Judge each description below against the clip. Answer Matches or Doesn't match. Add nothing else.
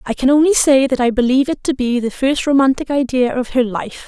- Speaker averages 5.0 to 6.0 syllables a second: Matches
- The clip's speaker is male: Doesn't match